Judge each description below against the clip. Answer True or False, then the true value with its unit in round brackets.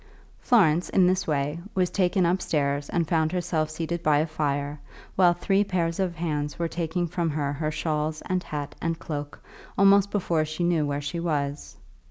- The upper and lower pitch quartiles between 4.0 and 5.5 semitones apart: False (2.9 semitones)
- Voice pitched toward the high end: False (165 Hz)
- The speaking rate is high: False (180 wpm)